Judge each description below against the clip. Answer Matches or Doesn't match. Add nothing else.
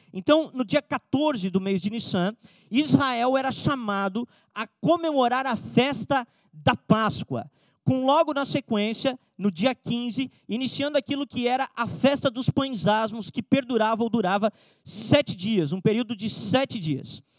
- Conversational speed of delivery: Matches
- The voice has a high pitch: Matches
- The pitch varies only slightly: Doesn't match